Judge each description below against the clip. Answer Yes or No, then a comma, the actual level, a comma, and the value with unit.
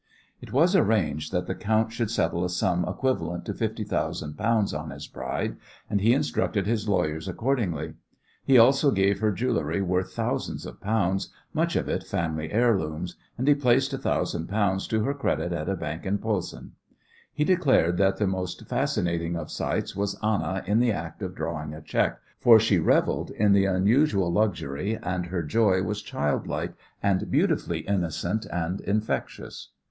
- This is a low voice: Yes, very low, 95 Hz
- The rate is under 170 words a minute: No, average, 175 wpm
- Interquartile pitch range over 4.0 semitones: Yes, average, 4.4 semitones